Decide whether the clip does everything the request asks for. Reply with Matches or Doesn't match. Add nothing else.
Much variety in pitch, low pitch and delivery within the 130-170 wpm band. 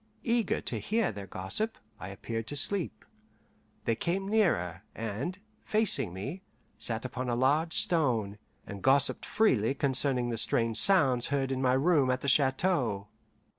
Matches